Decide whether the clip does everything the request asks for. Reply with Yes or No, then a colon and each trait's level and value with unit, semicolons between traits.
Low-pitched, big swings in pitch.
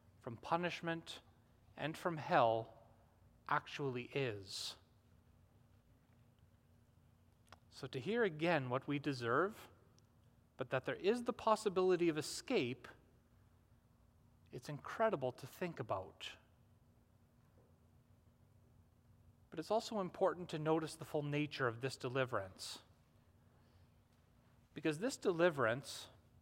Yes: low, 120 Hz; wide, 5.8 semitones